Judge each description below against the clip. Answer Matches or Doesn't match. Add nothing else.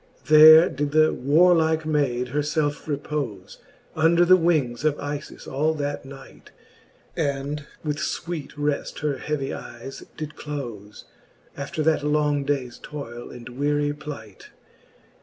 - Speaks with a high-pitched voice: Doesn't match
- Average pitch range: Doesn't match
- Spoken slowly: Matches